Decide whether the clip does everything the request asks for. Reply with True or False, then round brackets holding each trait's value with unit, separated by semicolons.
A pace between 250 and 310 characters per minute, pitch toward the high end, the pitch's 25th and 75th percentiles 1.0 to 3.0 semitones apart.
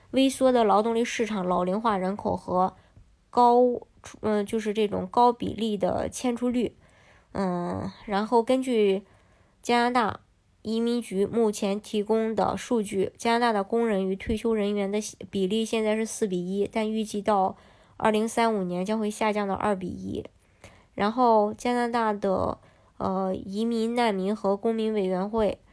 False (235 characters per minute; 215 Hz; 2.7 semitones)